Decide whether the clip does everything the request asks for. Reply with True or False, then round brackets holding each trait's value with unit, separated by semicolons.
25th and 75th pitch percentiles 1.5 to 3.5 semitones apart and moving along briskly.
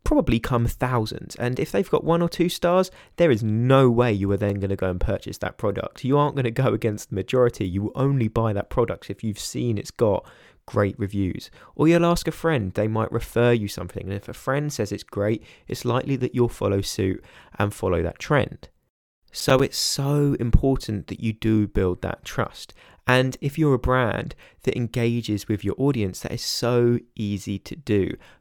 False (4.4 semitones; 210 wpm)